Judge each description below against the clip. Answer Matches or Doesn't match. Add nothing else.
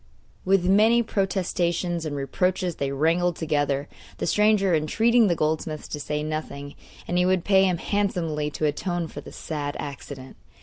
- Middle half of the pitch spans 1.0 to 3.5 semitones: Doesn't match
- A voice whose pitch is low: Doesn't match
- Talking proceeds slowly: Doesn't match